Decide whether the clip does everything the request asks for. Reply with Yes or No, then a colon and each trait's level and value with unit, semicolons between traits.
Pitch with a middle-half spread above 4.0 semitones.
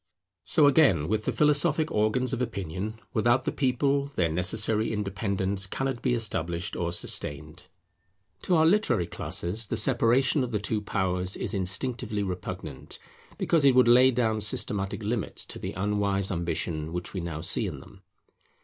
Yes: wide, 5.6 semitones